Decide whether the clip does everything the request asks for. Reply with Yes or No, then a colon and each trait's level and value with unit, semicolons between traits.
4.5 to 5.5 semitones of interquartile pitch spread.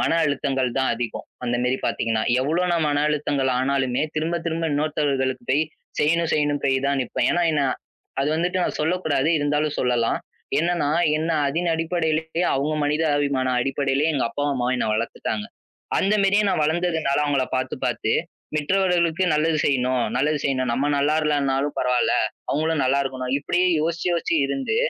No: average, 3.5 semitones